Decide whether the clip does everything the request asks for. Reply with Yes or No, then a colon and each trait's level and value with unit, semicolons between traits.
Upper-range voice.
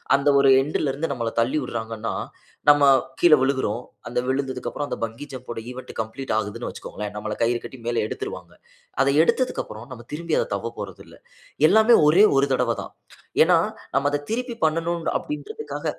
No: low, 130 Hz